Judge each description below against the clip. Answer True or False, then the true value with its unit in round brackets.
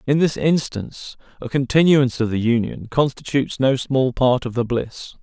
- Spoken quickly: False (170 wpm)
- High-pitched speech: False (130 Hz)